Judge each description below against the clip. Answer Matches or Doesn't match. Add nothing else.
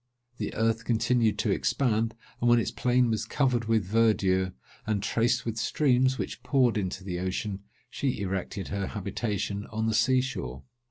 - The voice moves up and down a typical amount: Matches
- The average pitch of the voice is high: Doesn't match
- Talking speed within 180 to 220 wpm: Doesn't match